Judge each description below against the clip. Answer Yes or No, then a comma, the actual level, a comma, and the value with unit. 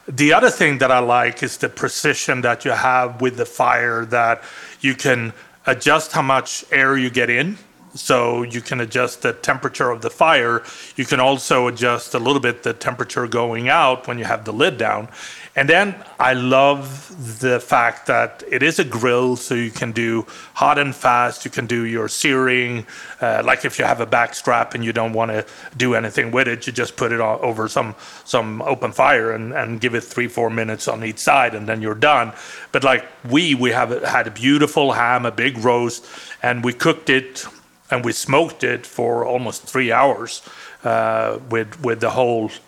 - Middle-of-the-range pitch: No, low, 125 Hz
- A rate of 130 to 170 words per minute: No, average, 200 wpm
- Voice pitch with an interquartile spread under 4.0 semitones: Yes, narrow, 2.4 semitones